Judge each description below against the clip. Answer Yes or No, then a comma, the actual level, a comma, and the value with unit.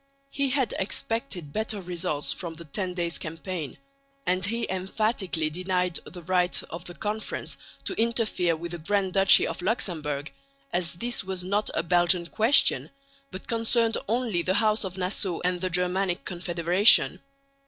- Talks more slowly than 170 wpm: Yes, average, 155 wpm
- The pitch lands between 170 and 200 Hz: Yes, medium, 185 Hz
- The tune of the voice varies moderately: Yes, average, 3.4 semitones